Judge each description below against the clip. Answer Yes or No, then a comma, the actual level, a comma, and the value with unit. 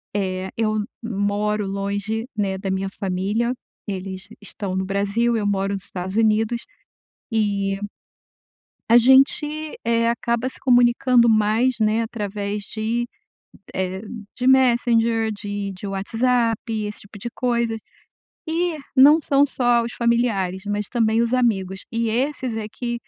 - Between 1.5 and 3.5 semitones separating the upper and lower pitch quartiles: Yes, average, 3.1 semitones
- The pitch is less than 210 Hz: No, high, 220 Hz